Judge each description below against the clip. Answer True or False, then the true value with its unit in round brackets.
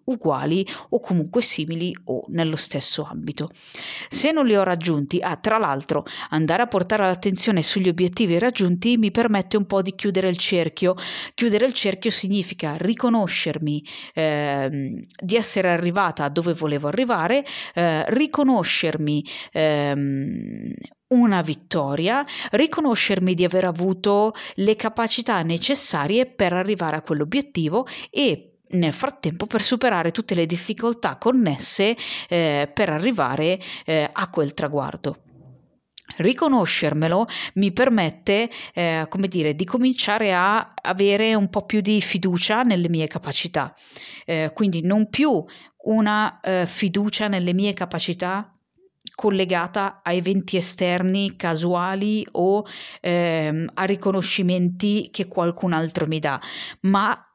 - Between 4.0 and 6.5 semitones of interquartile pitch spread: True (4.5 semitones)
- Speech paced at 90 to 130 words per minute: True (125 wpm)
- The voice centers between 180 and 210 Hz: True (190 Hz)